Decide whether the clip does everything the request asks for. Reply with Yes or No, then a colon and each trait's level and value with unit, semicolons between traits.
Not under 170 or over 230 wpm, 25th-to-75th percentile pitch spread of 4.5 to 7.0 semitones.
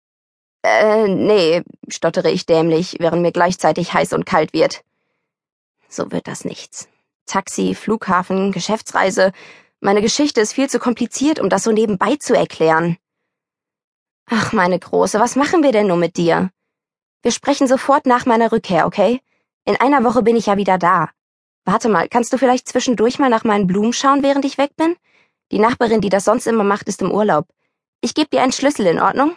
Yes: average, 180 wpm; average, 4.9 semitones